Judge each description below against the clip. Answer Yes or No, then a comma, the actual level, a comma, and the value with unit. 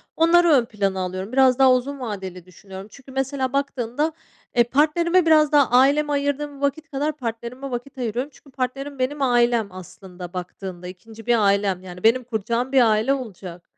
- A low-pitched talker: No, very high, 250 Hz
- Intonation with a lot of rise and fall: Yes, wide, 5.7 semitones